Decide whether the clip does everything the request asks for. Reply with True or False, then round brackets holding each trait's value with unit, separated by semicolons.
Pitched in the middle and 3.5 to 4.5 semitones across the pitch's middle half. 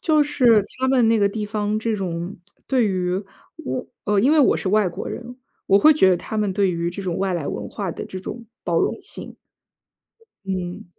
False (205 Hz; 3.8 semitones)